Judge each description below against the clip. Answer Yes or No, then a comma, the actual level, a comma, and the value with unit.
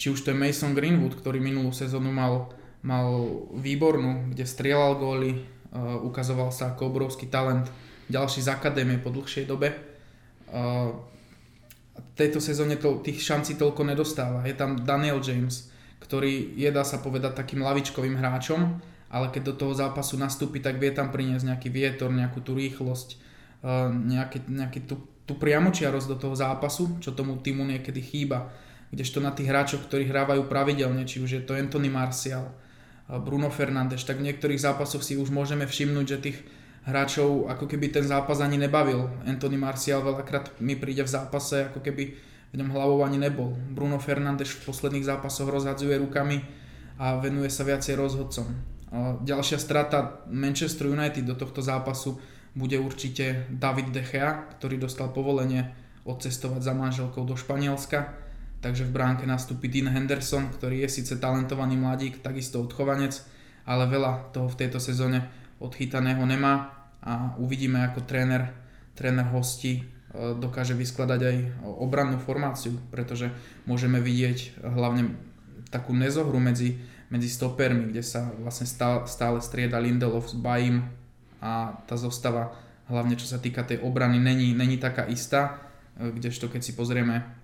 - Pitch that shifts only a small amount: Yes, narrow, 1.7 semitones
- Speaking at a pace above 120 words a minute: Yes, average, 150 wpm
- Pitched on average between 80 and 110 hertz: No, low, 130 Hz